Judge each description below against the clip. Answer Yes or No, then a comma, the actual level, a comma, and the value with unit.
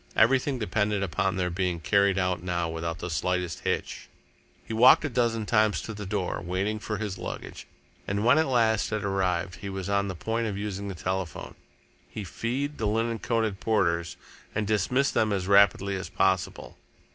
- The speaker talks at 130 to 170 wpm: No, average, 180 wpm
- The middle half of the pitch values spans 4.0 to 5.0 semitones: No, average, 3.2 semitones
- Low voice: Yes, low, 100 Hz